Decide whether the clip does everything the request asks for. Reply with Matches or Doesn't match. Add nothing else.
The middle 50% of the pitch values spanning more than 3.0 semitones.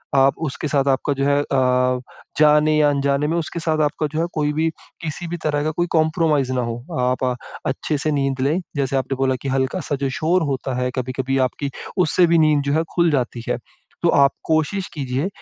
Doesn't match